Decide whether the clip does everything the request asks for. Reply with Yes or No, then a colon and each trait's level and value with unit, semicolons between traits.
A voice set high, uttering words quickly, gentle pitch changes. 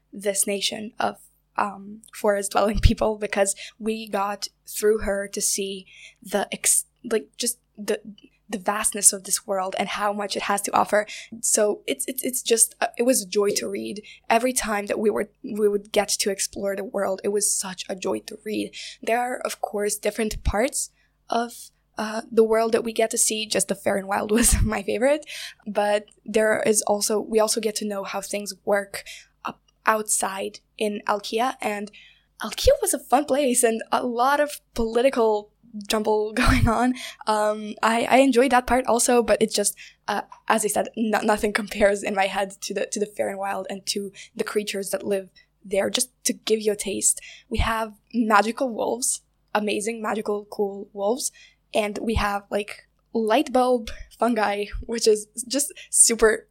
No: high, 215 Hz; average, 185 wpm; narrow, 2.3 semitones